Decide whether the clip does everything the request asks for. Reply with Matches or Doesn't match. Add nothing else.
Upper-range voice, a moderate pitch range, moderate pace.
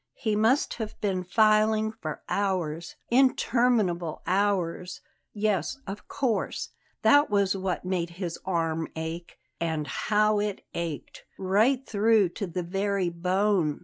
Doesn't match